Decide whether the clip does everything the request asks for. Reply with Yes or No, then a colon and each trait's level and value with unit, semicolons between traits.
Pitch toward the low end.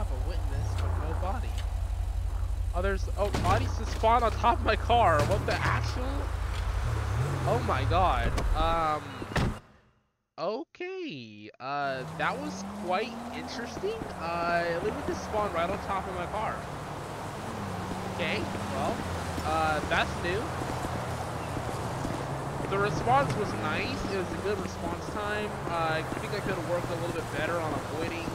Yes: low, 100 Hz